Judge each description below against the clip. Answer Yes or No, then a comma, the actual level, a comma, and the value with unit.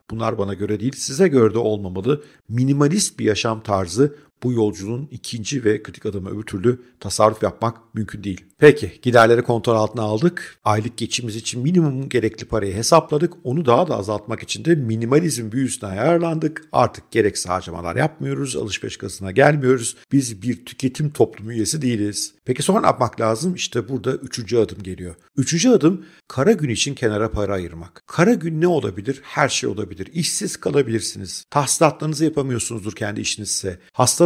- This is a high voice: No, low, 120 Hz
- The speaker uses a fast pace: Yes, fast, 160 wpm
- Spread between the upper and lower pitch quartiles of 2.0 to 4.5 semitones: No, average, 5.2 semitones